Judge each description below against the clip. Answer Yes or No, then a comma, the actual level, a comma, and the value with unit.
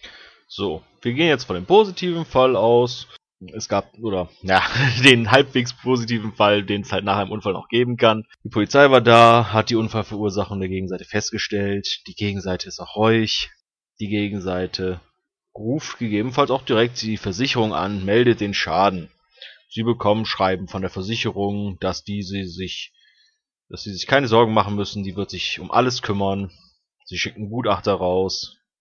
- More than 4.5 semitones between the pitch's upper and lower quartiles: No, average, 3.3 semitones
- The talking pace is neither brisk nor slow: Yes, average, 165 wpm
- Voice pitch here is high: No, low, 105 Hz